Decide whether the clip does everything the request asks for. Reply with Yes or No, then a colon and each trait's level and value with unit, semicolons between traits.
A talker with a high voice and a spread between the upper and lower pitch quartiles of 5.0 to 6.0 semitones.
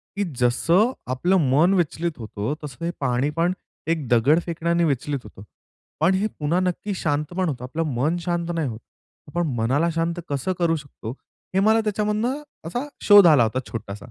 No: medium, 165 Hz; average, 5.3 semitones